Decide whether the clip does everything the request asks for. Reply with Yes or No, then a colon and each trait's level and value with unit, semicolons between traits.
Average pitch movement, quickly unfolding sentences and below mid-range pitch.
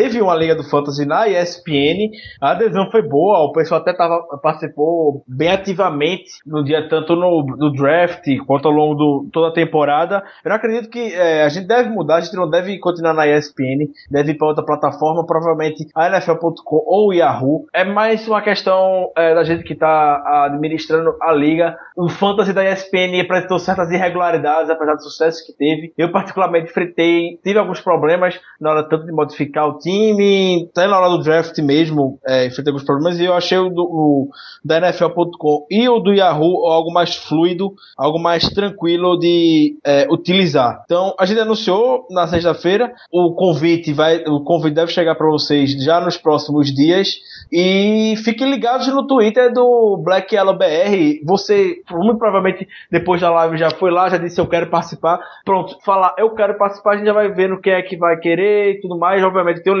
No: average, 3.4 semitones; fast, 190 wpm; medium, 170 Hz